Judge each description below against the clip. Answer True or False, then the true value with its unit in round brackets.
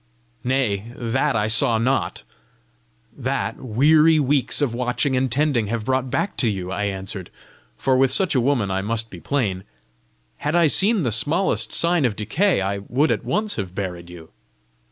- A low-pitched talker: True (125 Hz)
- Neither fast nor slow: True (175 wpm)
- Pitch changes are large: True (5.7 semitones)